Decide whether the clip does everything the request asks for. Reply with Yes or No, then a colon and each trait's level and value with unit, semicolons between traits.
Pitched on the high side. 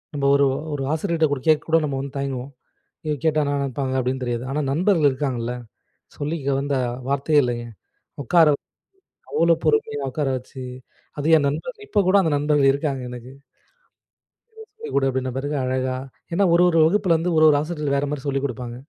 No: medium, 145 Hz